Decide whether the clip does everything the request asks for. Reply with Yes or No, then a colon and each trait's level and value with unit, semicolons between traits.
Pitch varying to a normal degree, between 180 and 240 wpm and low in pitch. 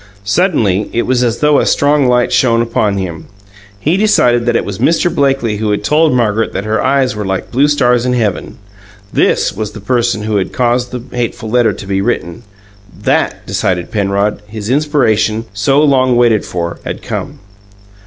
Yes: average, 3.8 semitones; average, 185 wpm; low, 120 Hz